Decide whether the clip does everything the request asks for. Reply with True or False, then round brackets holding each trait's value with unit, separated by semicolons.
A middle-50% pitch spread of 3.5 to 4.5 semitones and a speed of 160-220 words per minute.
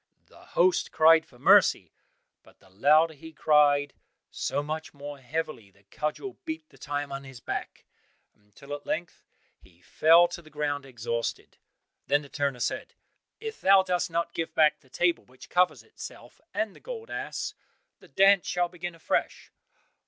True (3.8 semitones; 165 wpm)